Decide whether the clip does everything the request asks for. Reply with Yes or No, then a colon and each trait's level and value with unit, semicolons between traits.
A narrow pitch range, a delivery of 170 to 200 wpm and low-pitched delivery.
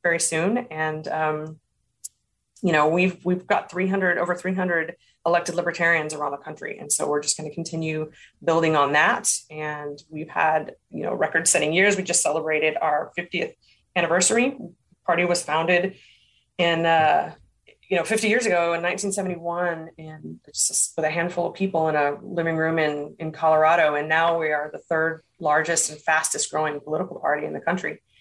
No: narrow, 2.2 semitones; average, 175 wpm; medium, 165 Hz